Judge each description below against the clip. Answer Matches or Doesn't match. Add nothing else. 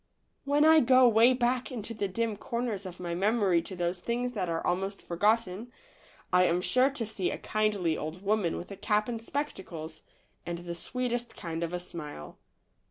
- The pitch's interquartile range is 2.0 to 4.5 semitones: Doesn't match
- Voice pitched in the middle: Doesn't match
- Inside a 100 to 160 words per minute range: Doesn't match